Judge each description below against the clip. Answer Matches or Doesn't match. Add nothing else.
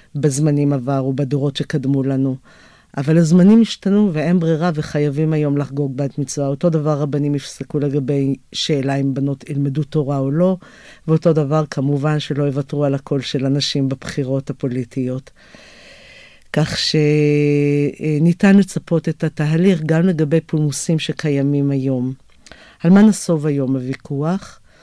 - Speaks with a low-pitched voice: Doesn't match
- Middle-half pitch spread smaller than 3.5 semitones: Matches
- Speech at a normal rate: Matches